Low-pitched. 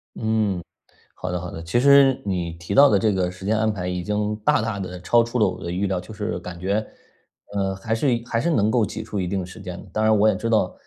Yes: low, 100 Hz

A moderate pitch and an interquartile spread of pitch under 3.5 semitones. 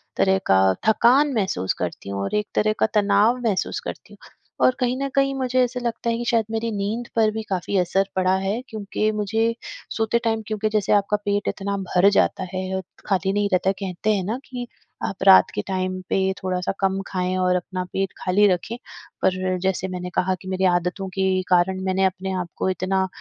No: high, 195 Hz; average, 2.7 semitones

